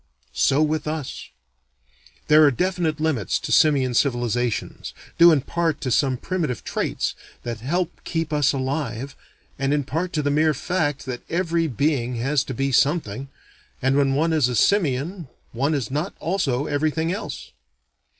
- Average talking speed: Yes, average, 160 wpm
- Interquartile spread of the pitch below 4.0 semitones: Yes, average, 3.4 semitones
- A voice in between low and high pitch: Yes, medium, 145 Hz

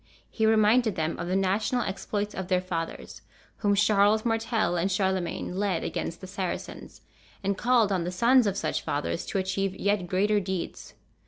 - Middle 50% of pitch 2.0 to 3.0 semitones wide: Yes, narrow, 2.6 semitones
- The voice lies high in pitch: Yes, high, 195 Hz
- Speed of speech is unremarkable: Yes, average, 170 wpm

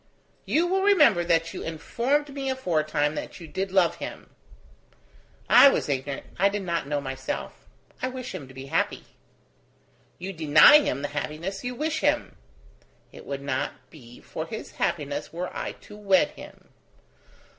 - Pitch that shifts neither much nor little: No, wide, 9.0 semitones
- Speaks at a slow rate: No, average, 160 wpm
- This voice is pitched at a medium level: Yes, medium, 170 Hz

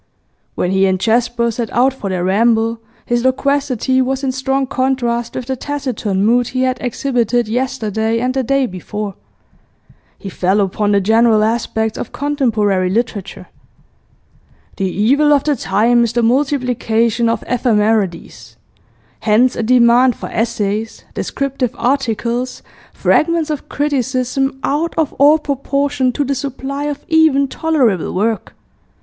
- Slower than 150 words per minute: Yes, average, 140 wpm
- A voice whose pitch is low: No, high, 245 Hz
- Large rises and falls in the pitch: No, average, 3.5 semitones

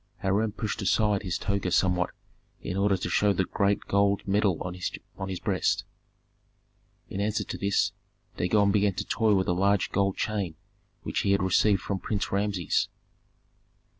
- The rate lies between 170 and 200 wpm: No, average, 160 wpm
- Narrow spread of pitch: Yes, narrow, 1.5 semitones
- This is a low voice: Yes, low, 100 Hz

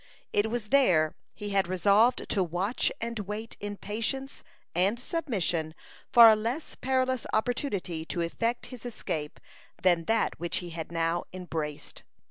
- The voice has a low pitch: No, high, 205 Hz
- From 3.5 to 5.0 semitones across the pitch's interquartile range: No, wide, 5.4 semitones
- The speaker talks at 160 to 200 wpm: No, average, 145 wpm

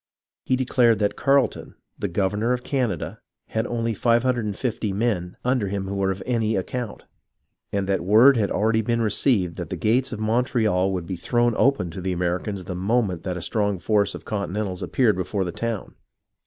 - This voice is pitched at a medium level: No, low, 105 Hz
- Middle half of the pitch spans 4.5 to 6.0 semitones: No, average, 3.9 semitones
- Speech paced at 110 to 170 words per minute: No, average, 180 wpm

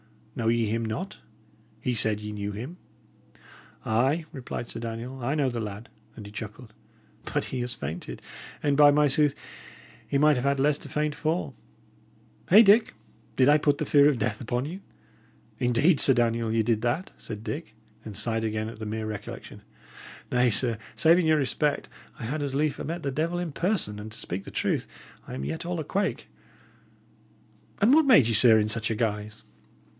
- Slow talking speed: No, average, 190 wpm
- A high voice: No, low, 125 Hz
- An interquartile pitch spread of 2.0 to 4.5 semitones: No, average, 5.3 semitones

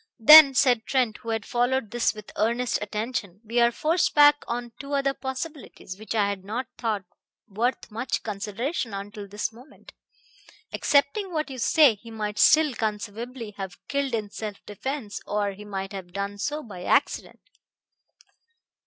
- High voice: Yes, high, 230 Hz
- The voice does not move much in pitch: No, average, 4.3 semitones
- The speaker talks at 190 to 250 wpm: No, average, 160 wpm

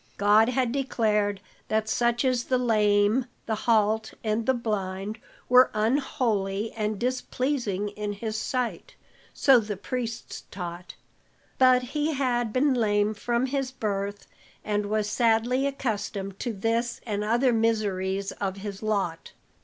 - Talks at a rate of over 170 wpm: No, slow, 135 wpm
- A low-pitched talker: No, high, 220 Hz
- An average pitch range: Yes, average, 3.3 semitones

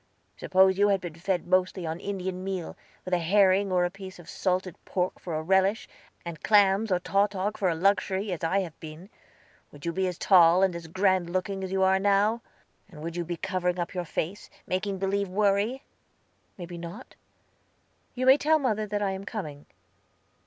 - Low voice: No, high, 190 Hz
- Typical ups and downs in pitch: No, narrow, 2.3 semitones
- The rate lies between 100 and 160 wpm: No, average, 195 wpm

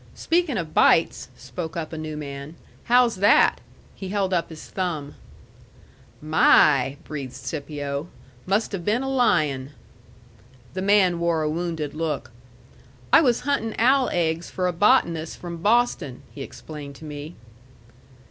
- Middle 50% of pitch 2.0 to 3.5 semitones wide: No, average, 5.1 semitones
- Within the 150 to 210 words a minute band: No, average, 140 wpm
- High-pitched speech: No, medium, 165 Hz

